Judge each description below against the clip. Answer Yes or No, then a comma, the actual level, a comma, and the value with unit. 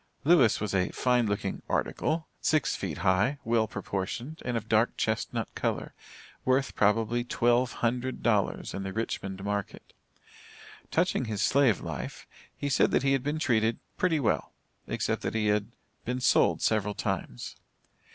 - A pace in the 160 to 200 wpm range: No, average, 150 wpm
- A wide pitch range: No, average, 4.0 semitones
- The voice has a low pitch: Yes, low, 115 Hz